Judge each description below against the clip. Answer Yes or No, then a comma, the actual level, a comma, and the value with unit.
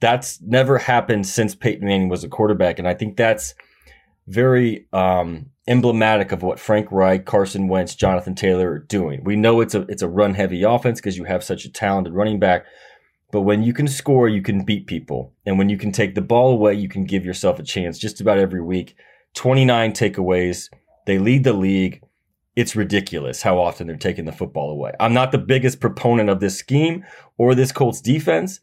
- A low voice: Yes, low, 105 Hz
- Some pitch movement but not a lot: Yes, average, 3.9 semitones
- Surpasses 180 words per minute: Yes, fast, 205 wpm